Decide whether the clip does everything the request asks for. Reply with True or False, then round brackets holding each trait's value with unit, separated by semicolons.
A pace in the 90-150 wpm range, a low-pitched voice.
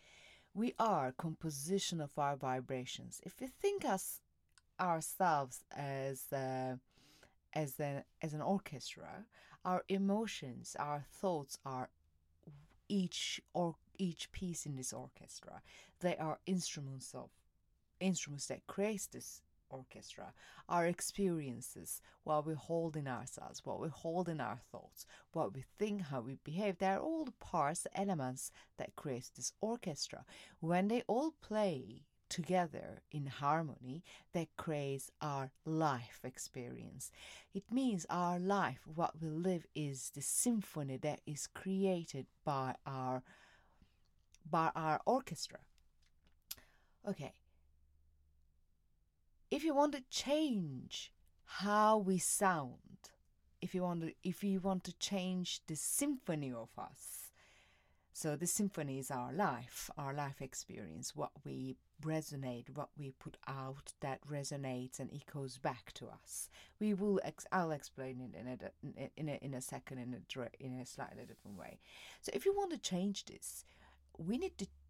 False (140 wpm; 150 Hz)